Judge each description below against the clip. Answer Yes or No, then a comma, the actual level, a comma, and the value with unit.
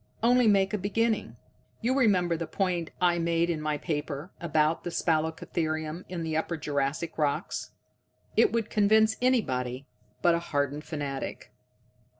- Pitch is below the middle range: No, medium, 170 Hz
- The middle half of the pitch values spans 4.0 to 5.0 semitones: Yes, average, 4.6 semitones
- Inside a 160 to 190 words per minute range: No, average, 140 wpm